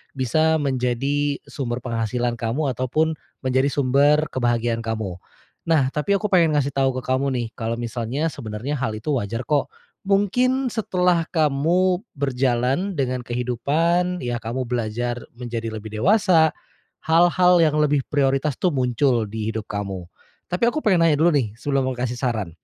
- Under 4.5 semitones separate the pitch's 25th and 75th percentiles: No, average, 4.9 semitones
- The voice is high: No, low, 135 Hz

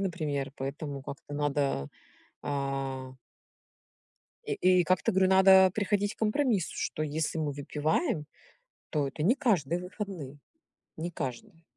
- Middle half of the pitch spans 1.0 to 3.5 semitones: No, average, 5.2 semitones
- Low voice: No, medium, 155 Hz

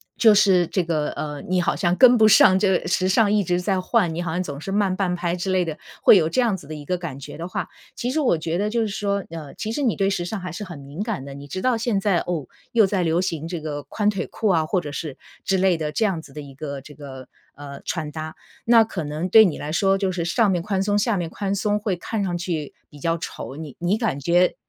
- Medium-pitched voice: Yes, medium, 180 Hz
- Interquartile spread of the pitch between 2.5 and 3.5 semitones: No, average, 4.4 semitones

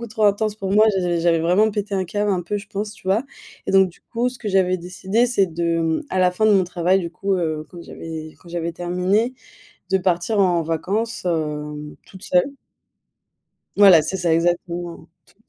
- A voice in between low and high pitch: Yes, medium, 180 Hz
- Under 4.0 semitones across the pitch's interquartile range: Yes, average, 3.2 semitones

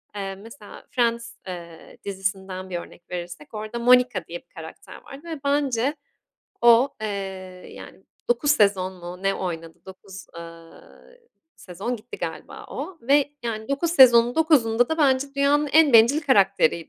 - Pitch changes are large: Yes, wide, 6.5 semitones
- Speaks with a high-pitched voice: Yes, high, 230 Hz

